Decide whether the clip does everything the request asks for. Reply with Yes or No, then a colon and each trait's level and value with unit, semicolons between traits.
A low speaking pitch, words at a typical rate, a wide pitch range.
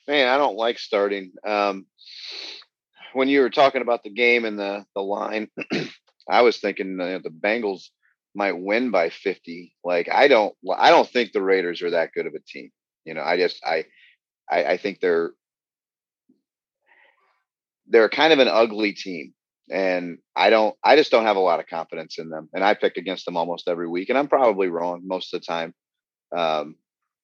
Yes: low, 100 Hz; average, 190 wpm; wide, 7.5 semitones